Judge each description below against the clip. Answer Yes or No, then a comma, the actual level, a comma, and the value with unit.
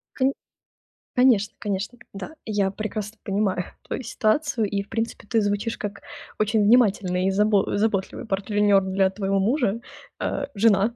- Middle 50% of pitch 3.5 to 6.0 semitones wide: No, narrow, 2.4 semitones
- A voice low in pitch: No, high, 205 Hz